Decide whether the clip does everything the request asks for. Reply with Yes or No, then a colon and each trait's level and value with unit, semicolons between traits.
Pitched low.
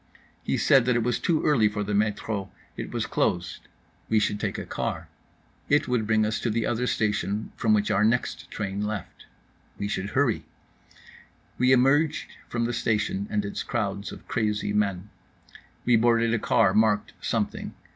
Yes: low, 110 Hz